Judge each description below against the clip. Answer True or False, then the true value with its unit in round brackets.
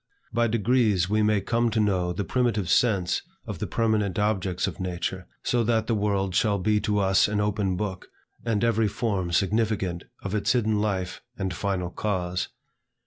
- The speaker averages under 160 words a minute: False (175 wpm)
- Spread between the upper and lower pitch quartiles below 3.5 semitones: True (2.7 semitones)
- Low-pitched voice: True (105 Hz)